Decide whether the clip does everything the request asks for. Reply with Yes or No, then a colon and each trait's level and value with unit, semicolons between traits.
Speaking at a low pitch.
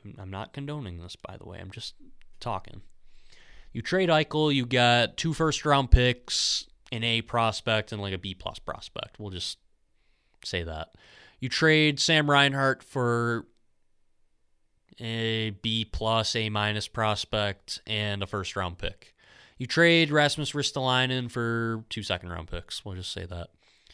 Yes: low, 110 Hz